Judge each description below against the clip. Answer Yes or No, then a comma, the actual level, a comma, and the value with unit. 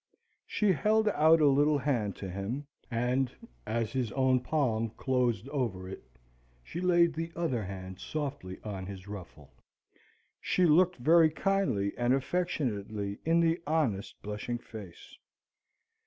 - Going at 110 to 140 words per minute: Yes, slow, 135 wpm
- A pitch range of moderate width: No, wide, 7.5 semitones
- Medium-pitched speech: No, low, 130 Hz